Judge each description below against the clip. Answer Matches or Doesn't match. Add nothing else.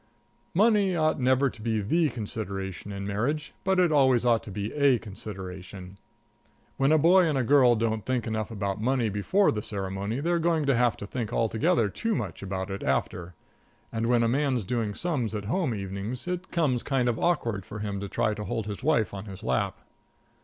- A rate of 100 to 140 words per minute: Doesn't match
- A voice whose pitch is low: Matches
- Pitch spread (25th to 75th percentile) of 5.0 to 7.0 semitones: Matches